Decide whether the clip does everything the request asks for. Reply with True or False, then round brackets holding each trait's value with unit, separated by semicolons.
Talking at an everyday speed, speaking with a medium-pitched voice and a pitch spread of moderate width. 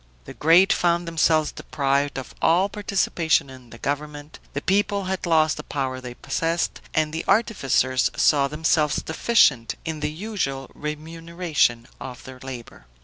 True (145 wpm; 155 Hz; 3.9 semitones)